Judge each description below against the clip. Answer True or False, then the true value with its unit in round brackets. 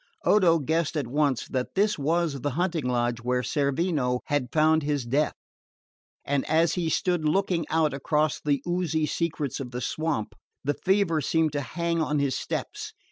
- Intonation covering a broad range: False (3.3 semitones)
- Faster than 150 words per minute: True (170 wpm)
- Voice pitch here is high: False (150 Hz)